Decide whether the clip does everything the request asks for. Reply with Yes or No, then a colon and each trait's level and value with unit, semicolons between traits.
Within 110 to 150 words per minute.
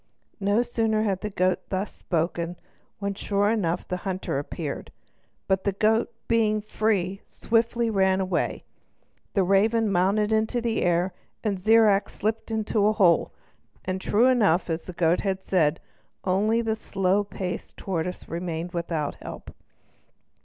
Yes: average, 145 wpm